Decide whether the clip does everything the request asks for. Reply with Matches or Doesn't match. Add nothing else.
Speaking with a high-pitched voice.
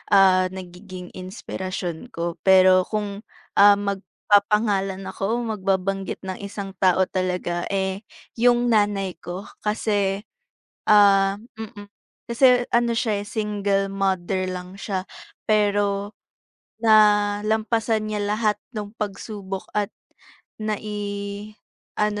Matches